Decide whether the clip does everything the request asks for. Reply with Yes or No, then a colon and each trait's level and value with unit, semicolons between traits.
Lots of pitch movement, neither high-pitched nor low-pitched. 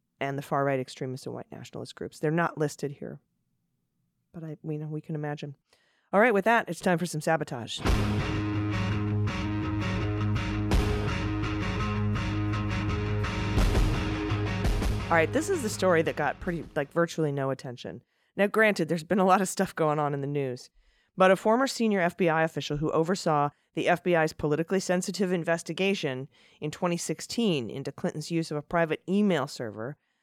Yes: wide, 8.5 semitones; medium, 150 Hz